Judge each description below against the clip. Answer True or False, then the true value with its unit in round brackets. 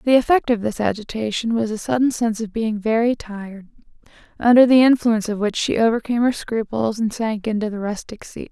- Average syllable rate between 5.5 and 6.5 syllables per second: True (5.9 syllables/s)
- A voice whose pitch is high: True (225 Hz)